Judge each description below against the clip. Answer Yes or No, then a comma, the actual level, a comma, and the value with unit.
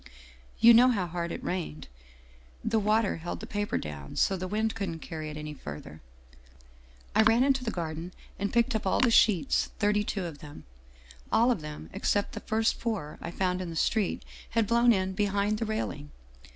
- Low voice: No, high, 200 Hz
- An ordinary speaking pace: Yes, average, 195 wpm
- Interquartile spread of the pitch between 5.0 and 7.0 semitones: Yes, average, 5.3 semitones